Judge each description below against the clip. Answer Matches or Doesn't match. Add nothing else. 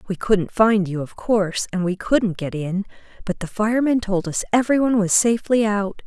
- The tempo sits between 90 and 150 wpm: Doesn't match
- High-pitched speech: Matches